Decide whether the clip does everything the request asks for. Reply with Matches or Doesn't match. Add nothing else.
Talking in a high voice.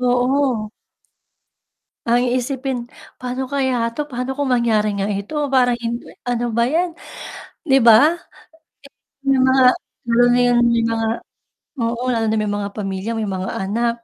Matches